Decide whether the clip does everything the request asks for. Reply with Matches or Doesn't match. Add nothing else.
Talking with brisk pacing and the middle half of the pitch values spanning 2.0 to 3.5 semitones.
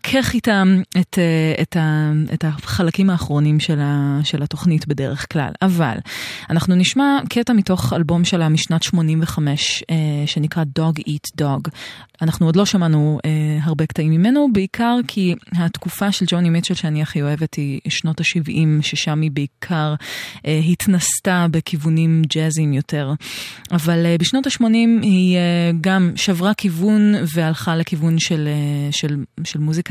Doesn't match